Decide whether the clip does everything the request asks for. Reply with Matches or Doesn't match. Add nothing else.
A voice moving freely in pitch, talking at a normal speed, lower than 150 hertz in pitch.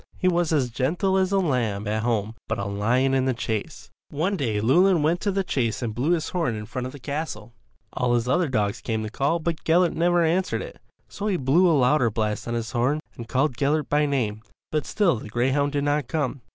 Doesn't match